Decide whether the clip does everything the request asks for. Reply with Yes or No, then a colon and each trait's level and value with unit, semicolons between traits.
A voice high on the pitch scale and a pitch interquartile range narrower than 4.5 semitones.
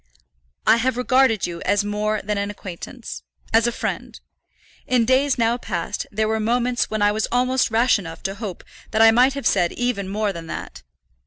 Yes: high, 220 Hz; average, 3.4 semitones